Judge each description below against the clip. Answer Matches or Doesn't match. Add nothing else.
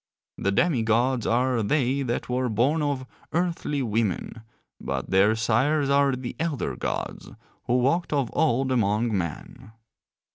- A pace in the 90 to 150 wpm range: Matches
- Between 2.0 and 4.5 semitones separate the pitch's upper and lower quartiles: Matches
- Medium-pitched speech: Doesn't match